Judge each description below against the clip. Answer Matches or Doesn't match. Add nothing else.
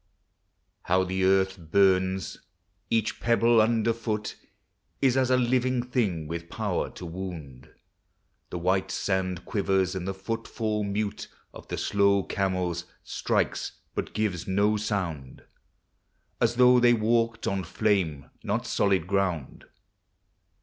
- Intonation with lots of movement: Doesn't match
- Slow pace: Matches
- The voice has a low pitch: Matches